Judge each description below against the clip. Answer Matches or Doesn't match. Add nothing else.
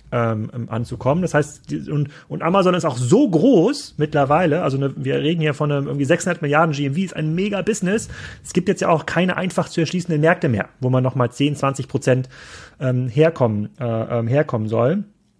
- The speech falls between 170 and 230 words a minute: Matches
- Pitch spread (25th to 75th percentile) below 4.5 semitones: Doesn't match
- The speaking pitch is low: Doesn't match